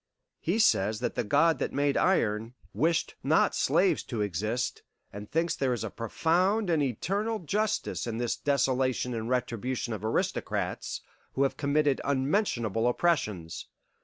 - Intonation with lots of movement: Yes, wide, 6.4 semitones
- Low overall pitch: Yes, low, 130 Hz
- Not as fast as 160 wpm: Yes, average, 145 wpm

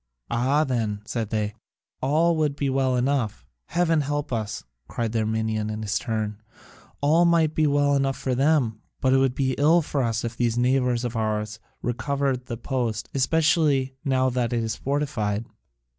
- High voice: No, low, 130 Hz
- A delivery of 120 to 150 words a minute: No, average, 175 wpm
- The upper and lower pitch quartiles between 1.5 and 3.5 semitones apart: No, average, 4.2 semitones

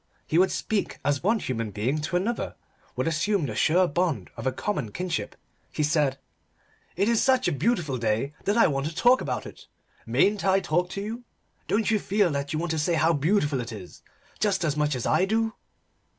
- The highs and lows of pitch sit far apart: Yes, wide, 6.1 semitones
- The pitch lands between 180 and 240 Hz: No, medium, 170 Hz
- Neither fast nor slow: No, fast, 210 wpm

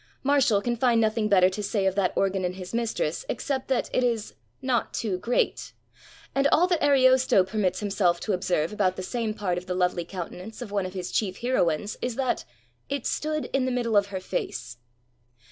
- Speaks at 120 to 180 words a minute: No, fast, 205 wpm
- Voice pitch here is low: No, high, 210 Hz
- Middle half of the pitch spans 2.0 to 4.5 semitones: No, average, 5.0 semitones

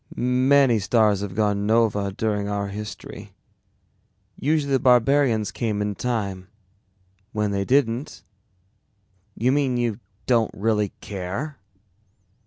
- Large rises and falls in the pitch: No, average, 3.6 semitones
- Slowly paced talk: Yes, slow, 115 wpm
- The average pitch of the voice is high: No, low, 110 Hz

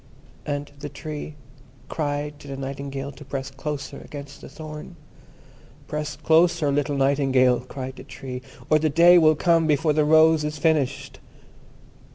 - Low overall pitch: No, medium, 145 Hz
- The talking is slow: No, average, 150 wpm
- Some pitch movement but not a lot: No, narrow, 2.1 semitones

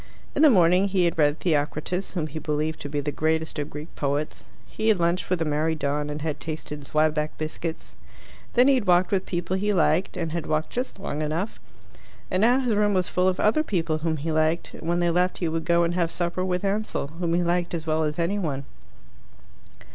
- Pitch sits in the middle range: Yes, medium, 170 Hz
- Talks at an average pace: No, fast, 225 wpm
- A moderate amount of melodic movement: Yes, average, 3.0 semitones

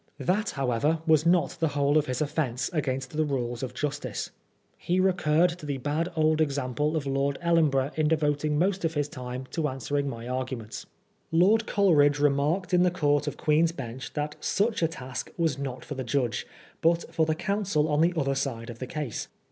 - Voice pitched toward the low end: No, medium, 150 Hz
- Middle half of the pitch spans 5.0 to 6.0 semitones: No, average, 3.5 semitones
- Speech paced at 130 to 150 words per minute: No, average, 195 wpm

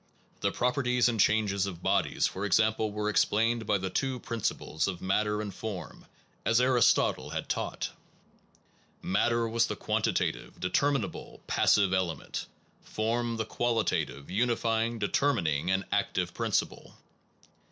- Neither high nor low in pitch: No, low, 110 Hz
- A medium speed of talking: No, slow, 130 wpm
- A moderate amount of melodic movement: Yes, average, 3.2 semitones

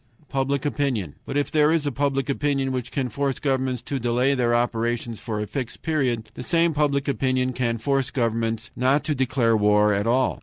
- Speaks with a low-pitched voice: Yes, low, 130 Hz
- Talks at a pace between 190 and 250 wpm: Yes, average, 195 wpm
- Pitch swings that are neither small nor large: Yes, average, 3.1 semitones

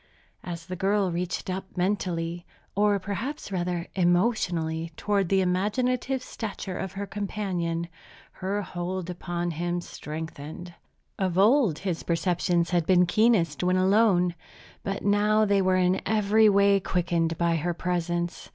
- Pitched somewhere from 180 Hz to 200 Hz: Yes, medium, 185 Hz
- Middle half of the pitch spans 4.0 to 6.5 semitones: No, average, 2.7 semitones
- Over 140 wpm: No, slow, 135 wpm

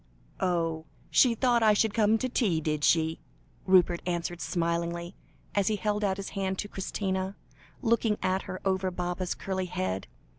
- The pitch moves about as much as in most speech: Yes, average, 3.2 semitones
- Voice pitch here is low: No, high, 190 Hz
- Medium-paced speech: Yes, average, 160 wpm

